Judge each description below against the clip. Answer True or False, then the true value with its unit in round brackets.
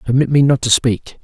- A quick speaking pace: True (240 wpm)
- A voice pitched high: False (125 Hz)